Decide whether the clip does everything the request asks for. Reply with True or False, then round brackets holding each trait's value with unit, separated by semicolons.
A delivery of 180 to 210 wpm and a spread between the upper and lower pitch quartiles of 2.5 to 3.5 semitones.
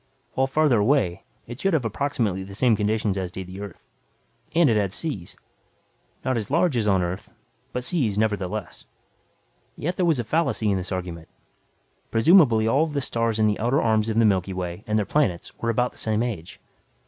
False (195 wpm; 5.0 semitones)